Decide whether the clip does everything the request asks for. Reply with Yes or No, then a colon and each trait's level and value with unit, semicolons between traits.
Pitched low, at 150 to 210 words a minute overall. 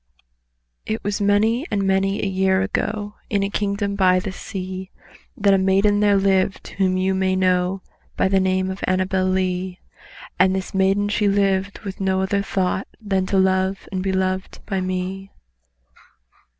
No: high, 190 Hz; average, 165 wpm